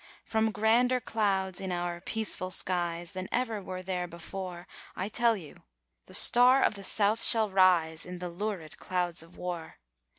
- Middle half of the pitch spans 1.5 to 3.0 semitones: No, average, 3.7 semitones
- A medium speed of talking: Yes, average, 165 wpm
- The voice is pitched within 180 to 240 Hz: Yes, medium, 185 Hz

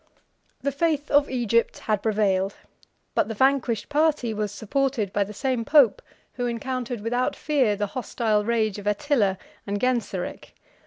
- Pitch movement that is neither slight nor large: Yes, average, 4.2 semitones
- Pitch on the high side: Yes, high, 230 Hz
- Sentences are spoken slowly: No, average, 155 wpm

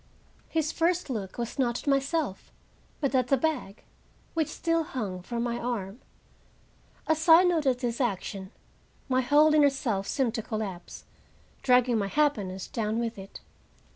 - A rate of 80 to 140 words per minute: No, average, 150 wpm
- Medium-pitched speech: No, very high, 250 Hz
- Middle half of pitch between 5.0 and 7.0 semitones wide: Yes, wide, 5.5 semitones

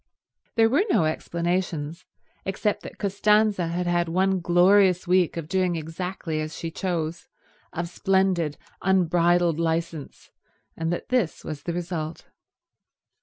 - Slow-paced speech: Yes, slow, 125 wpm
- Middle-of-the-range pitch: Yes, medium, 175 Hz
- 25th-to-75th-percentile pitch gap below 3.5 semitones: Yes, narrow, 2.5 semitones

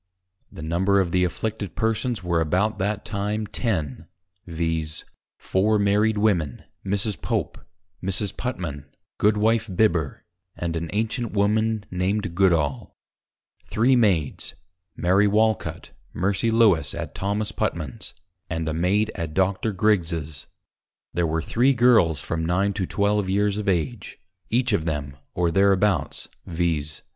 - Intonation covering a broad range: No, average, 4.4 semitones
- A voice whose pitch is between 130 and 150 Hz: No, very low, 95 Hz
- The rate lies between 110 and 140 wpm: Yes, slow, 135 wpm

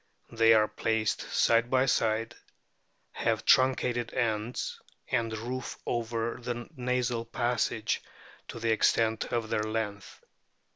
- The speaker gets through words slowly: Yes, slow, 115 wpm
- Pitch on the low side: Yes, low, 115 Hz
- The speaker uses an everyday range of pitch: No, narrow, 1.5 semitones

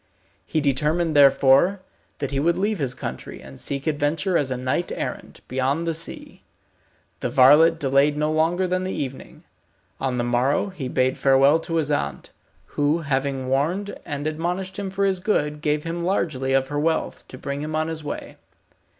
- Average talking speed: Yes, average, 180 wpm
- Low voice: No, medium, 150 Hz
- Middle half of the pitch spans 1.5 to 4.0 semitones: Yes, average, 3.7 semitones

